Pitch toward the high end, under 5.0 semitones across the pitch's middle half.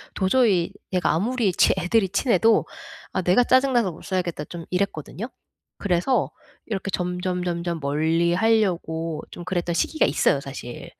No: medium, 180 Hz; average, 4.0 semitones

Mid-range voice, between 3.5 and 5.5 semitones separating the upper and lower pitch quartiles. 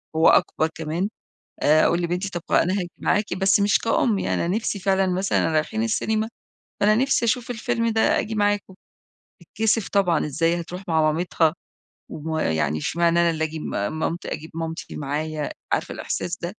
Yes: medium, 175 Hz; average, 4.5 semitones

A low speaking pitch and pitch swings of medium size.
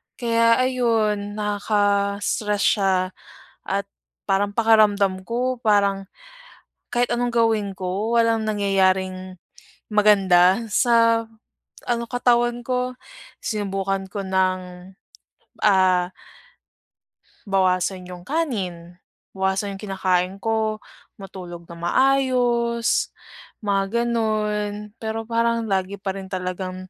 No: high, 205 Hz; average, 3.3 semitones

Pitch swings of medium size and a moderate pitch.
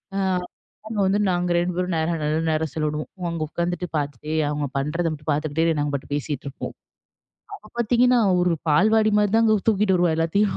Yes: average, 4.8 semitones; medium, 170 Hz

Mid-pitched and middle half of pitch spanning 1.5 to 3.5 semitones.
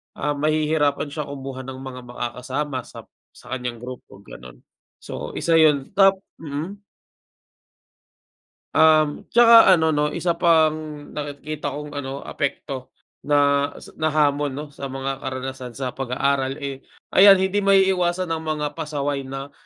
Yes: medium, 145 Hz; average, 2.8 semitones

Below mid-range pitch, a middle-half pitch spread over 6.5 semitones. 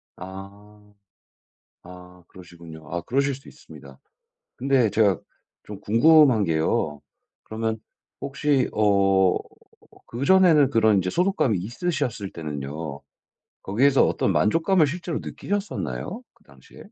Yes: low, 110 Hz; wide, 7.3 semitones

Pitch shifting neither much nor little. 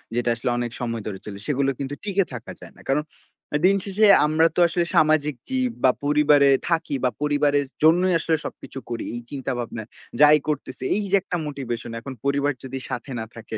Yes: average, 4.4 semitones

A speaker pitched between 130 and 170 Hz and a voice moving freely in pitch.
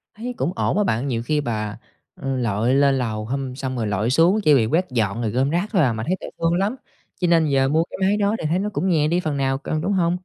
Yes: medium, 140 Hz; wide, 6.5 semitones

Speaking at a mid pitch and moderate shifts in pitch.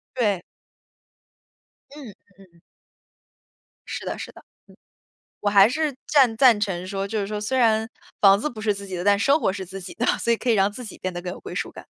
No: high, 205 Hz; average, 3.4 semitones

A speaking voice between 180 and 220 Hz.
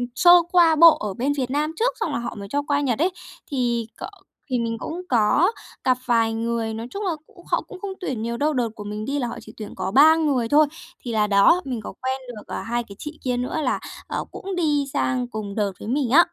No: very high, 250 Hz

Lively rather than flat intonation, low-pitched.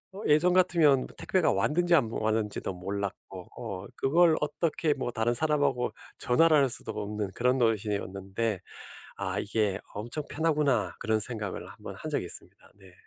Yes: wide, 6.5 semitones; low, 120 Hz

